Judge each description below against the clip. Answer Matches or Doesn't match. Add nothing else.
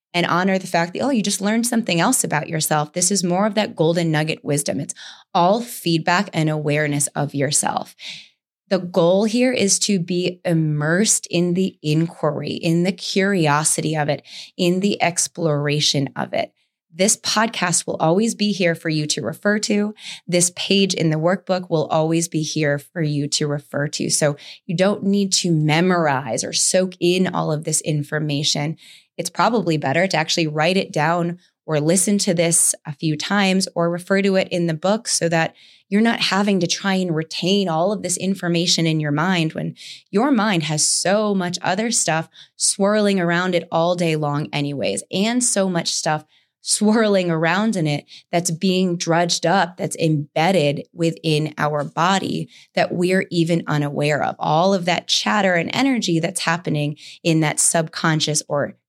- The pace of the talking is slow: Doesn't match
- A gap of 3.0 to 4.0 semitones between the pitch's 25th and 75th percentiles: Matches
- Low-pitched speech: Doesn't match